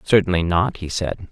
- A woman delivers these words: No, male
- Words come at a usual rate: Yes, average, 185 wpm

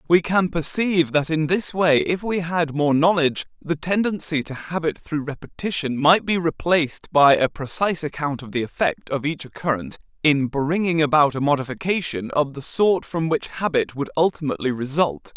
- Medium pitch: Yes, medium, 155 Hz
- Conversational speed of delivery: Yes, average, 175 wpm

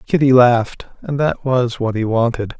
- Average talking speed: Yes, average, 185 wpm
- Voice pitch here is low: Yes, low, 125 Hz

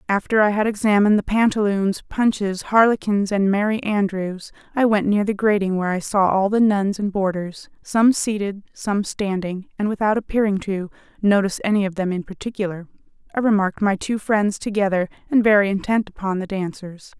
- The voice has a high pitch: Yes, high, 200 Hz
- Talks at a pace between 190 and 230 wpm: No, average, 175 wpm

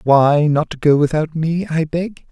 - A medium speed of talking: Yes, average, 180 wpm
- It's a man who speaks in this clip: Yes, male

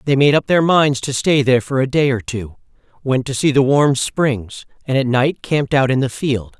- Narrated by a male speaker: Yes, male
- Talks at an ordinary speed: No, fast, 245 wpm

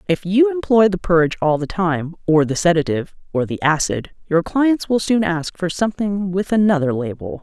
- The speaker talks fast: No, average, 195 wpm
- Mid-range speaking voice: Yes, medium, 180 Hz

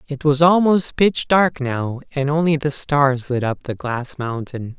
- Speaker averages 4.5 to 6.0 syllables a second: No, 4.0 syllables/s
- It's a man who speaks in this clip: Yes, male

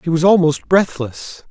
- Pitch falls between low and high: Yes, medium, 165 Hz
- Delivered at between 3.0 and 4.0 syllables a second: No, 4.2 syllables/s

